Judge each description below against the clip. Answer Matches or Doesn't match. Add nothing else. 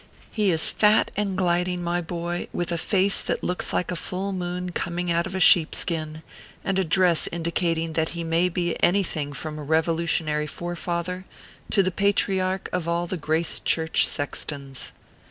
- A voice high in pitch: Doesn't match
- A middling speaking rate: Matches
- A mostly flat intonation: Matches